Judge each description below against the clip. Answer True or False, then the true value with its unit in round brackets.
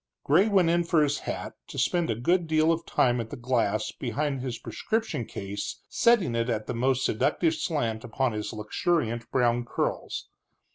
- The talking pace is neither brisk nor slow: True (180 wpm)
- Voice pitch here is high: False (130 Hz)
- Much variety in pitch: True (6.1 semitones)